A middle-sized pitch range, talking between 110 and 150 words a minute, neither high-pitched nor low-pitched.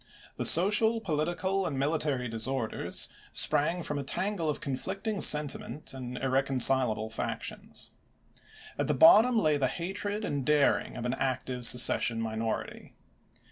No: wide, 5.9 semitones; slow, 135 wpm; medium, 145 Hz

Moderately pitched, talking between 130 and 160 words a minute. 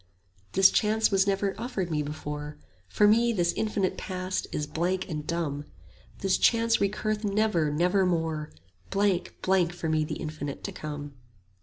Yes: medium, 180 Hz; average, 150 wpm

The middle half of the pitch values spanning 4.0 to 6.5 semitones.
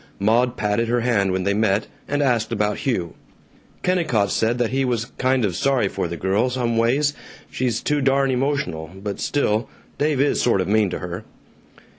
Yes: average, 4.6 semitones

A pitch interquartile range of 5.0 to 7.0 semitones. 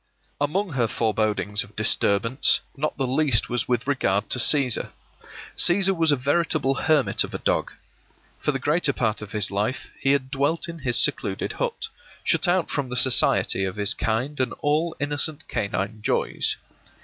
Yes: wide, 5.6 semitones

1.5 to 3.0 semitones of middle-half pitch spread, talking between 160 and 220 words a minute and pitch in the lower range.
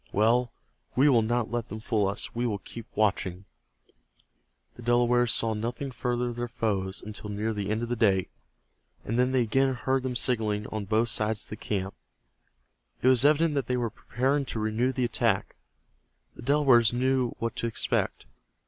Yes: narrow, 2.6 semitones; average, 185 wpm; low, 120 Hz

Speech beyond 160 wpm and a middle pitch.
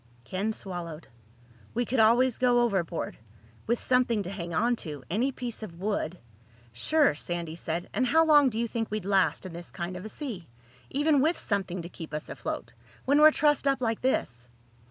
No: average, 175 wpm; high, 210 Hz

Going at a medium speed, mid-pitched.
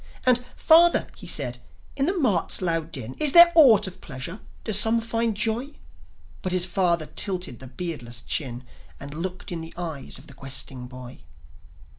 Yes: average, 170 wpm; medium, 180 Hz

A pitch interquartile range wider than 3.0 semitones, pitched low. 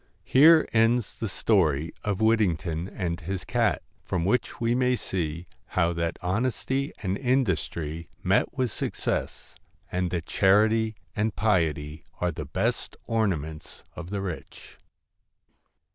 Yes: average, 5.1 semitones; very low, 95 Hz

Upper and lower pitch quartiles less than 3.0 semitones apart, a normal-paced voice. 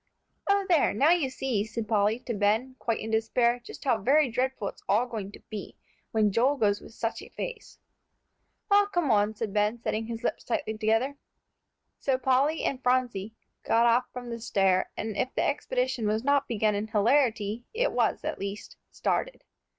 No: average, 3.7 semitones; average, 185 wpm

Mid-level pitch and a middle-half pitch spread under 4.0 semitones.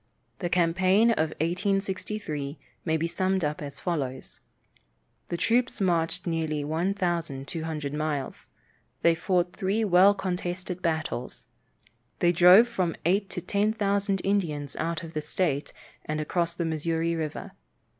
Yes: medium, 170 Hz; average, 3.3 semitones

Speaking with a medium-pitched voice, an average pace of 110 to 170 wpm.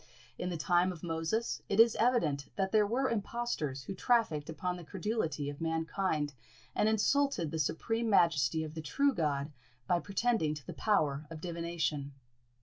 Yes: medium, 170 Hz; average, 165 wpm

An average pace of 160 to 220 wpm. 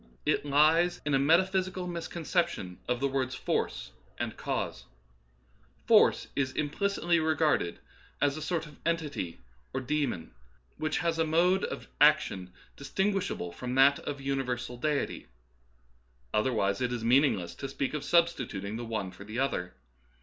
Yes: average, 170 wpm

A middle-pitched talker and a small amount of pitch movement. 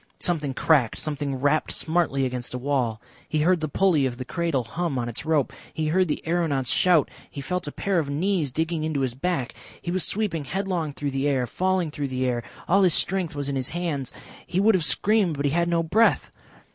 No: medium, 155 Hz; average, 4.4 semitones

